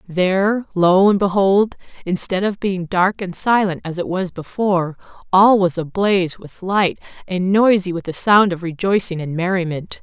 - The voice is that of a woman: Yes, female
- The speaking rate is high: No, average, 170 wpm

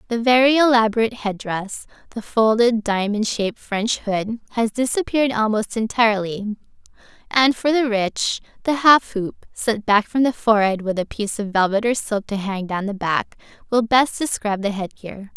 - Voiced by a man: No, female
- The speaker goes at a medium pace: Yes, average, 175 wpm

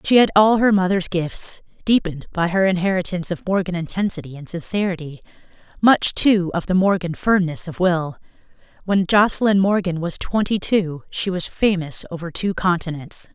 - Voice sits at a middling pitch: Yes, medium, 180 Hz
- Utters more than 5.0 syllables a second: Yes, 5.2 syllables/s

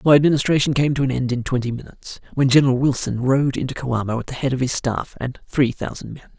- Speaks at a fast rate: Yes, fast, 235 wpm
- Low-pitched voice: Yes, low, 130 Hz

